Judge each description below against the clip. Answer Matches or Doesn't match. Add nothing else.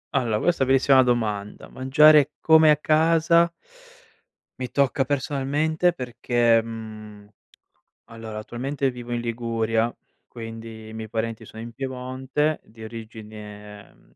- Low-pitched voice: Matches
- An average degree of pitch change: Matches